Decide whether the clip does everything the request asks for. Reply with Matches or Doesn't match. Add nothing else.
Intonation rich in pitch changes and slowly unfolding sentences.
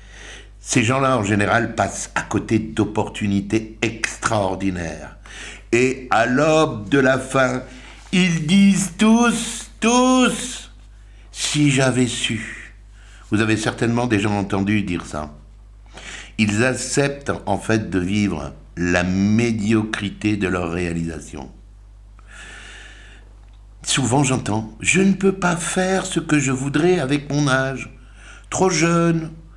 Matches